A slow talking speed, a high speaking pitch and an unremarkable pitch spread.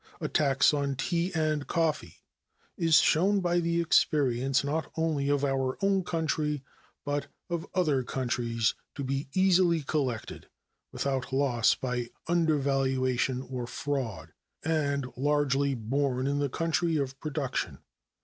No: slow, 130 wpm; medium, 140 Hz; average, 3.4 semitones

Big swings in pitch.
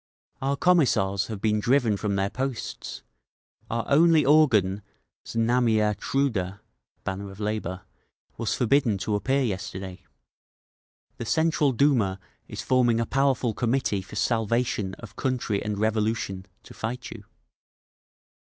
No: average, 4.6 semitones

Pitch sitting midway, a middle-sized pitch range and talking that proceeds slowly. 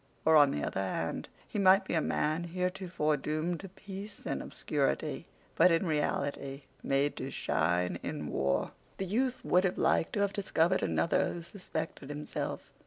No: medium, 165 Hz; average, 4.6 semitones; average, 170 wpm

